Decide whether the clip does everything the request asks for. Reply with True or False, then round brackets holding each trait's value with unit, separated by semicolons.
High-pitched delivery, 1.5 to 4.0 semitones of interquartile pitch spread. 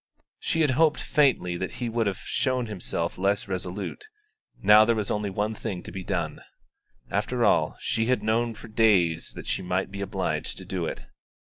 False (105 Hz; 3.7 semitones)